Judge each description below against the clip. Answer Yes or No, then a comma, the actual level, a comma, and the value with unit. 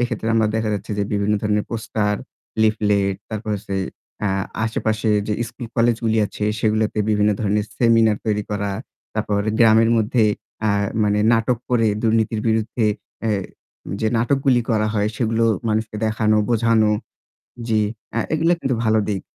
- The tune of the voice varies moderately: No, narrow, 1.4 semitones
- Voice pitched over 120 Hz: No, low, 110 Hz